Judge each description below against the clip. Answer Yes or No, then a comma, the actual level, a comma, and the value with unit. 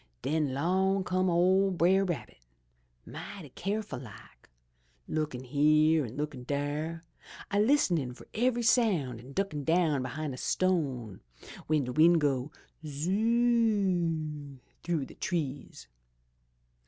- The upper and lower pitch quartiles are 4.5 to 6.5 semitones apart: Yes, average, 5.2 semitones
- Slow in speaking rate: Yes, slow, 120 wpm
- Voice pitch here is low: No, medium, 155 Hz